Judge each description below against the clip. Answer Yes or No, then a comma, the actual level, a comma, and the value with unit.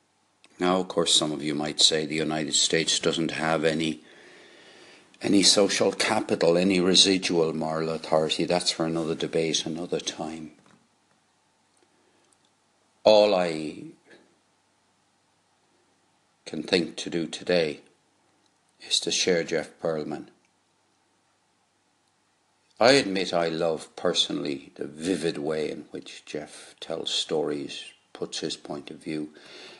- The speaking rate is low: Yes, slow, 115 wpm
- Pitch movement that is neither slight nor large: No, narrow, 2.3 semitones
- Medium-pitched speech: No, very low, 80 Hz